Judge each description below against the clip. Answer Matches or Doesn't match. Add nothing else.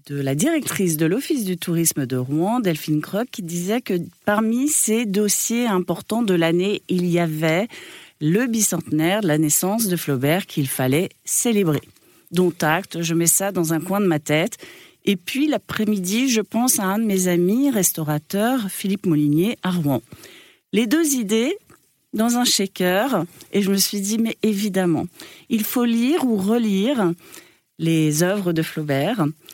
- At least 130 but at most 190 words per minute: Matches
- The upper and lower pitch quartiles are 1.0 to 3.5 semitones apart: Doesn't match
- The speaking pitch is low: Doesn't match